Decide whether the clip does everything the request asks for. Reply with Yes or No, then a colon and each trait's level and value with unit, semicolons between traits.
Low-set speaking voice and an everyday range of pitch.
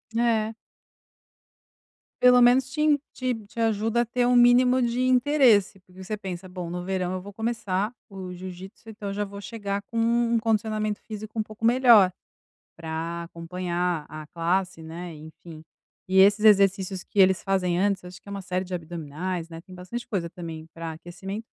No: high, 195 Hz; average, 4.0 semitones